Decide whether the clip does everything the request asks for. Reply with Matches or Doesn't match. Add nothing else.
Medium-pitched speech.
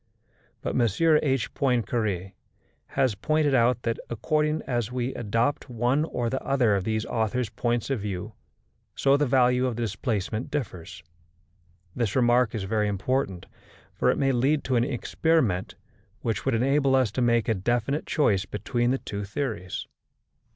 Doesn't match